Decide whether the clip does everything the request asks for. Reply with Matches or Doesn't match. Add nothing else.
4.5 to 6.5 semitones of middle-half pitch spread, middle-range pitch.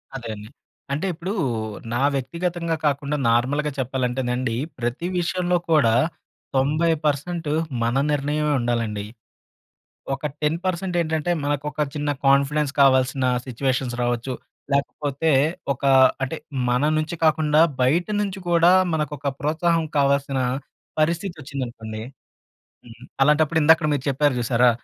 Doesn't match